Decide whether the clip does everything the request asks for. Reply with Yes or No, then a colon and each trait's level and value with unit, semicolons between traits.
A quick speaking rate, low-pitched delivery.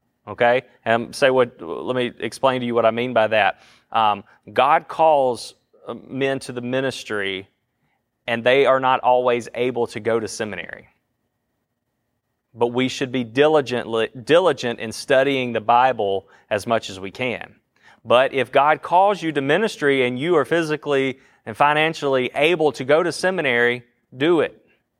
No: average, 160 wpm; low, 125 Hz